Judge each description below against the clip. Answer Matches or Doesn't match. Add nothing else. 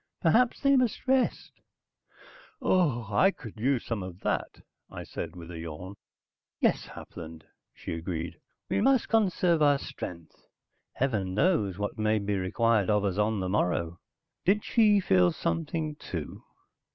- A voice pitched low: Matches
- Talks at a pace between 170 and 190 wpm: Doesn't match